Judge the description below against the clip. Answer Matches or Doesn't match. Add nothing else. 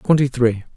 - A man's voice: Matches